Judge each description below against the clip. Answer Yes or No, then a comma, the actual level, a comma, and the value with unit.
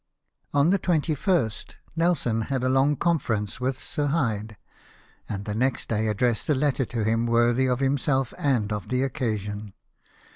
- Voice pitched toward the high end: No, low, 125 Hz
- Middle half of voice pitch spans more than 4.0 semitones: Yes, average, 4.4 semitones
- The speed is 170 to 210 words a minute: No, average, 155 wpm